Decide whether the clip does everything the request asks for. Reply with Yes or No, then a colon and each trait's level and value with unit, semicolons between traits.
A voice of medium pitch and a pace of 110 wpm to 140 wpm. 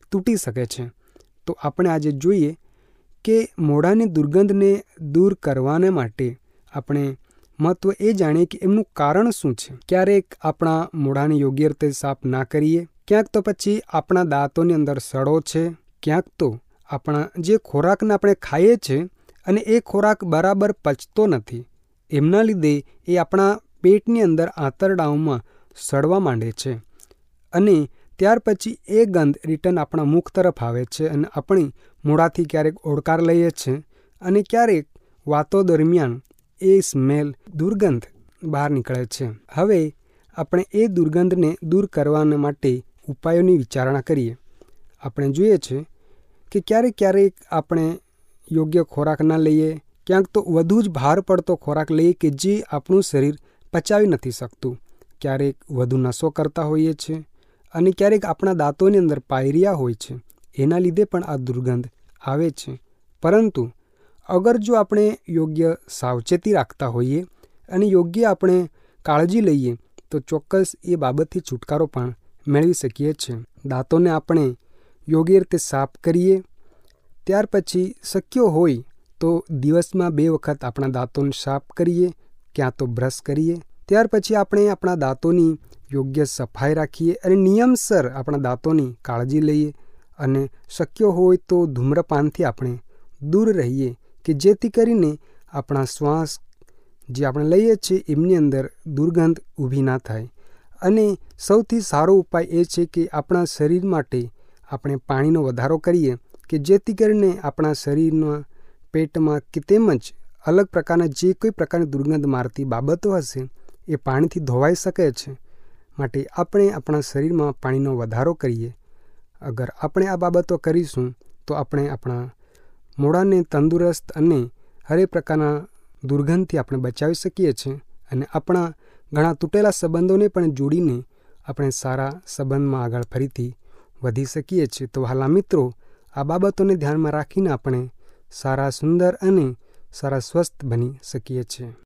Yes: medium, 155 Hz; average, 135 wpm